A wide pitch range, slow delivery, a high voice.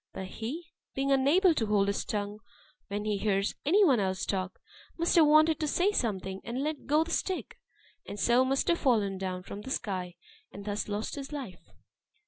No: wide, 7.1 semitones; average, 195 wpm; high, 230 Hz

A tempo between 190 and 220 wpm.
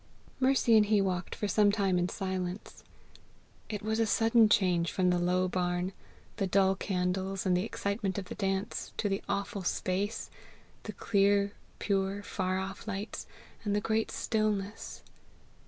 No: average, 155 wpm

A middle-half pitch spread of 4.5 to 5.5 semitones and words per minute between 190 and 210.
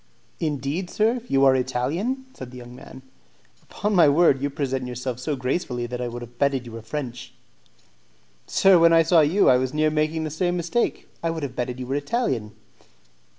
Yes: average, 4.8 semitones; average, 195 wpm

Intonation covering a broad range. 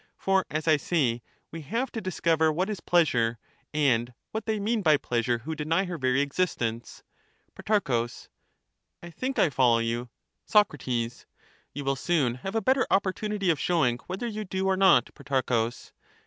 Yes: wide, 7.5 semitones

